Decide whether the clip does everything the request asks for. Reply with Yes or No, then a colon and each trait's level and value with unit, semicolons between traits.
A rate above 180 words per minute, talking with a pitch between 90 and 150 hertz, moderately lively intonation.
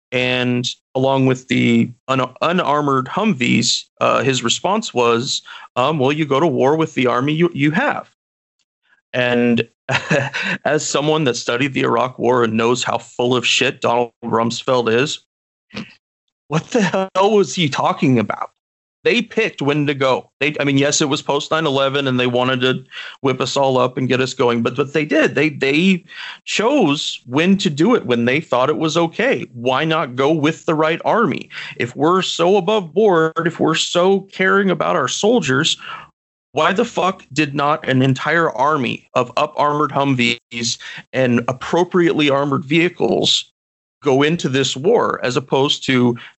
No: average, 170 wpm; medium, 140 Hz; average, 4.5 semitones